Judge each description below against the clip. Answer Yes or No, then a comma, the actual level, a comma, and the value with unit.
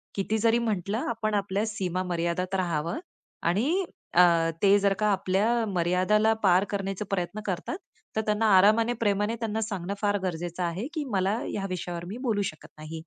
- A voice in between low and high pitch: No, high, 195 Hz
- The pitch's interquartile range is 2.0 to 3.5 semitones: Yes, average, 3.1 semitones